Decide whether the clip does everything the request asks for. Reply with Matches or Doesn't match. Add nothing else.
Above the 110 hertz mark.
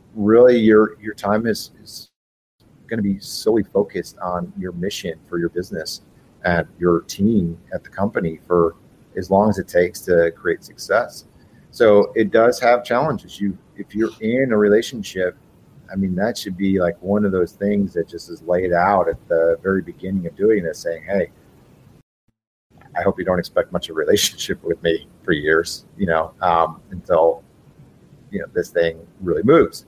Doesn't match